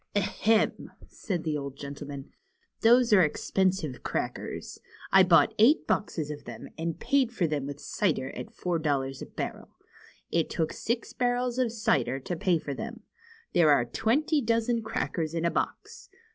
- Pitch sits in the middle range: Yes, medium, 175 Hz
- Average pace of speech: Yes, average, 165 wpm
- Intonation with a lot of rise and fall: Yes, wide, 7.5 semitones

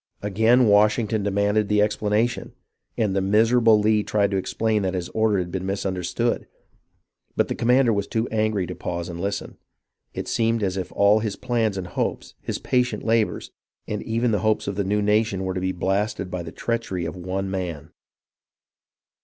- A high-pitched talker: No, low, 105 Hz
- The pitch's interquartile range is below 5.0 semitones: Yes, average, 2.7 semitones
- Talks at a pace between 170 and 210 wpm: Yes, average, 185 wpm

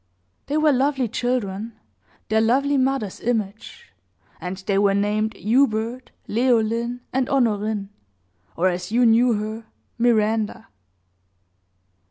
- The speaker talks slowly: Yes, slow, 110 wpm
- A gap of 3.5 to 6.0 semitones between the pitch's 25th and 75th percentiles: No, average, 3.1 semitones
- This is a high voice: Yes, high, 225 Hz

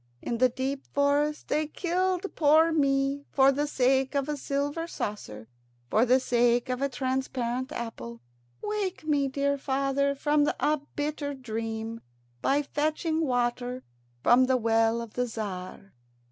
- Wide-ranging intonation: No, average, 3.3 semitones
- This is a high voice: Yes, very high, 270 Hz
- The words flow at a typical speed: Yes, average, 145 wpm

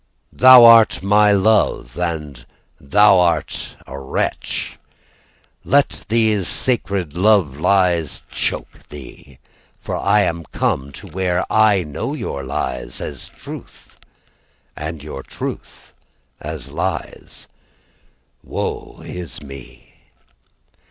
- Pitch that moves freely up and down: Yes, wide, 6.3 semitones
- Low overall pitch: Yes, very low, 90 Hz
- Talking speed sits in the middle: No, slow, 105 wpm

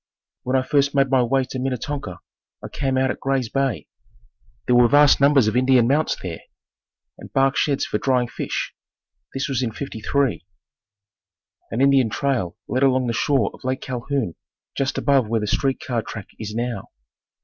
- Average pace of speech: Yes, average, 175 wpm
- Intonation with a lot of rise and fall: No, average, 2.7 semitones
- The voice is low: Yes, low, 130 Hz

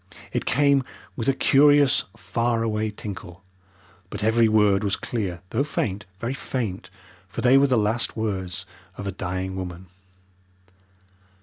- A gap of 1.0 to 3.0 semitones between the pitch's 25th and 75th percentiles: No, average, 4.5 semitones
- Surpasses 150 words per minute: No, slow, 135 wpm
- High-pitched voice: No, low, 110 Hz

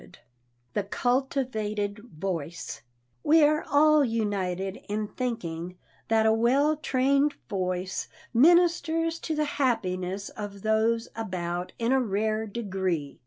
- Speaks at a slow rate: Yes, slow, 120 wpm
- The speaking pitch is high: Yes, high, 220 Hz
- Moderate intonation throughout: No, wide, 5.8 semitones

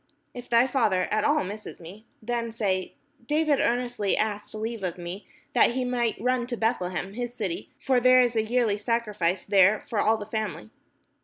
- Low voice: No, high, 220 Hz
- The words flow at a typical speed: Yes, average, 185 wpm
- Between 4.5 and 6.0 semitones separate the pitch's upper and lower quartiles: No, average, 3.2 semitones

